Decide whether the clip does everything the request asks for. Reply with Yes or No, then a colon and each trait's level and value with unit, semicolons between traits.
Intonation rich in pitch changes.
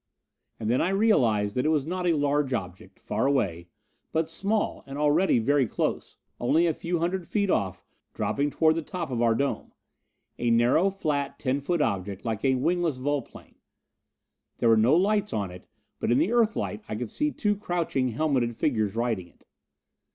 Yes: wide, 6.7 semitones